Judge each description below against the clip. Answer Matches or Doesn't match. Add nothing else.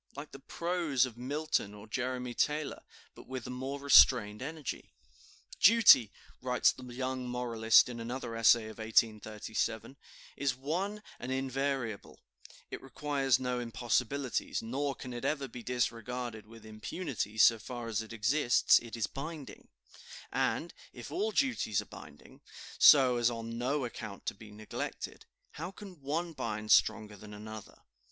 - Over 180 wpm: Doesn't match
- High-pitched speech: Doesn't match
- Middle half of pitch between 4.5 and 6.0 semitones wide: Doesn't match